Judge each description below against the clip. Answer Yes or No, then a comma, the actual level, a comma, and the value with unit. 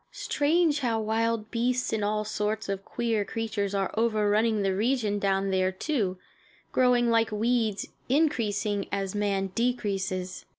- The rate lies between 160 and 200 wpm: No, slow, 135 wpm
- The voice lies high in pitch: Yes, high, 215 Hz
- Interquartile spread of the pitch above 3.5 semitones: No, average, 2.9 semitones